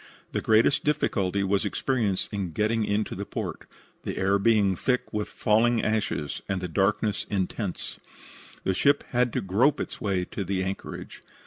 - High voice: No, low, 105 Hz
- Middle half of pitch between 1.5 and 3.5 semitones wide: Yes, average, 2.9 semitones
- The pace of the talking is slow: No, average, 155 wpm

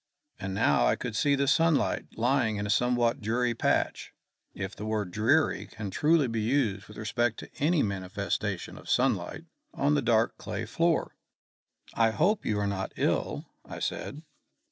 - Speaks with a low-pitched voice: Yes, low, 115 Hz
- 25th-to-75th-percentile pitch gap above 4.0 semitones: Yes, average, 5.1 semitones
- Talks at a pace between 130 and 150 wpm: No, average, 165 wpm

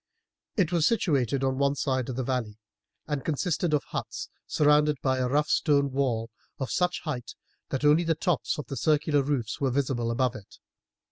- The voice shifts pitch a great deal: No, average, 2.8 semitones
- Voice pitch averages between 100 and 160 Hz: Yes, medium, 140 Hz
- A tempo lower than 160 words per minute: No, average, 185 wpm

